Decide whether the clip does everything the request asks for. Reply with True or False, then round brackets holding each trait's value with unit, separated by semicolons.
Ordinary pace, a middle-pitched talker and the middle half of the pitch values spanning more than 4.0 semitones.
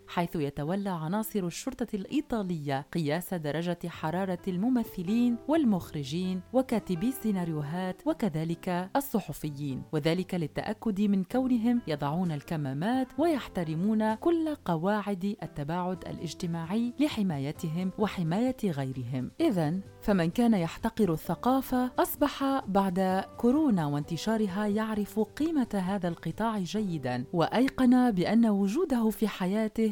False (95 wpm; 200 Hz; 5.4 semitones)